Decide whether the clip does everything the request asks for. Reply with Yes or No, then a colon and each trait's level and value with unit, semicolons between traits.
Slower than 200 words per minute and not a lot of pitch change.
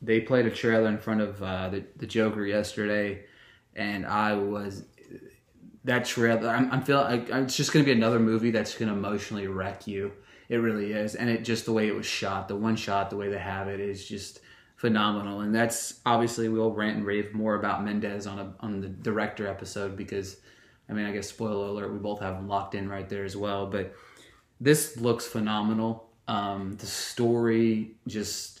No: fast, 205 wpm; narrow, 2.2 semitones